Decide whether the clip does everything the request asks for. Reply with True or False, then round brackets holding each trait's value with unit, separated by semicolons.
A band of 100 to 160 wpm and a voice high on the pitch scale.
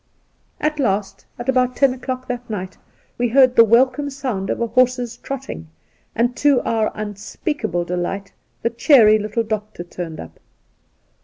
True (150 wpm; 235 Hz)